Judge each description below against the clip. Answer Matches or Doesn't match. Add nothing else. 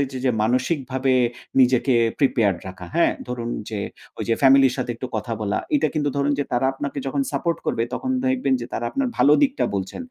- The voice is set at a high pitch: Doesn't match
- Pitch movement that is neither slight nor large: Matches